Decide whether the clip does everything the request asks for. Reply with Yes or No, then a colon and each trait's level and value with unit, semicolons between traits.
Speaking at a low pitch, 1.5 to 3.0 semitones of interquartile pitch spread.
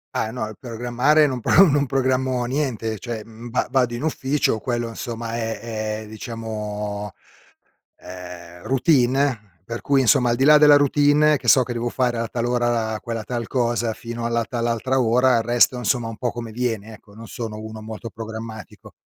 Yes: low, 120 Hz; narrow, 2.5 semitones